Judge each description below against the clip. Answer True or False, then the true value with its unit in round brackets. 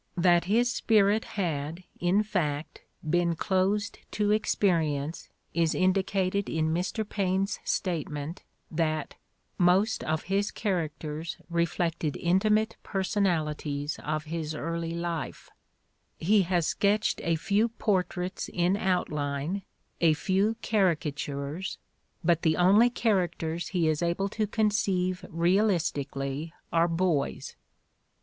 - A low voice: False (175 Hz)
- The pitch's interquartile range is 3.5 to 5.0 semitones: True (3.8 semitones)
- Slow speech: True (115 wpm)